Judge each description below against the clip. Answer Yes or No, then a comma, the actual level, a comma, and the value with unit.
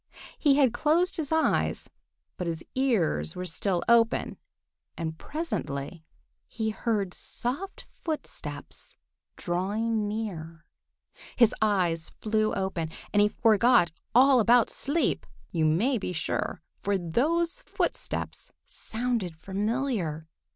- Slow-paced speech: Yes, slow, 110 wpm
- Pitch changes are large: Yes, wide, 6.4 semitones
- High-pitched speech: Yes, high, 215 Hz